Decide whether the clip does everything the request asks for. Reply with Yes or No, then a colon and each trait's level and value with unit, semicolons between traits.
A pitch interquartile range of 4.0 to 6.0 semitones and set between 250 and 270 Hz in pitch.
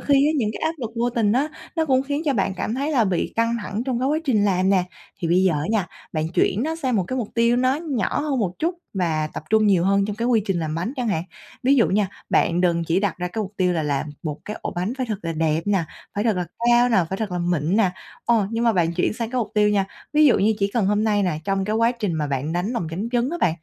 No: average, 5.1 semitones; high, 210 Hz